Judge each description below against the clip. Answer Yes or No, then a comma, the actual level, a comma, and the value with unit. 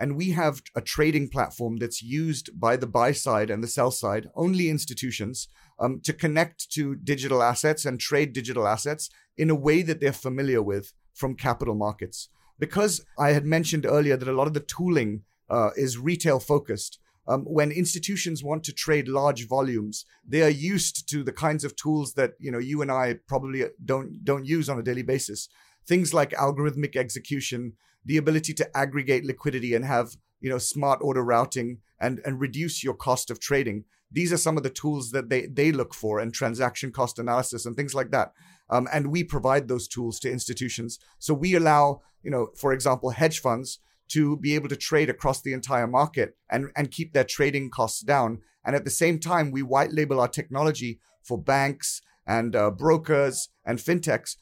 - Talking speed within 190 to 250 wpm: Yes, average, 195 wpm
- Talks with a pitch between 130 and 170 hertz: Yes, medium, 140 Hz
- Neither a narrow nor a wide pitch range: Yes, average, 3.5 semitones